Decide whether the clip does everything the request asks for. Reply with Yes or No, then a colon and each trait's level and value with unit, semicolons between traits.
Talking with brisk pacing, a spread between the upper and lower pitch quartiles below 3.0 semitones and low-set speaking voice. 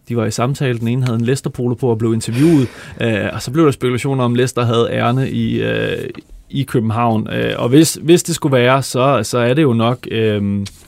Yes: fast, 230 wpm; narrow, 2.6 semitones; low, 125 Hz